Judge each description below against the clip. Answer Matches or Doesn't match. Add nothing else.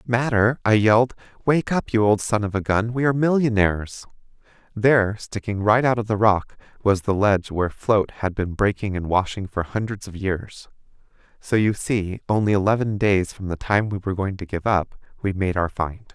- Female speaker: Doesn't match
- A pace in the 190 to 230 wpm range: Matches